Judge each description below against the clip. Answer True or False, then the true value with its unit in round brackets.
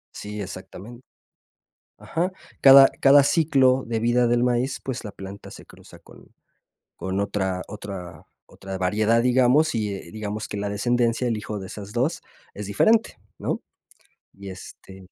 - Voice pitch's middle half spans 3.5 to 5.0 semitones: True (4.2 semitones)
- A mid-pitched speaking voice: False (110 Hz)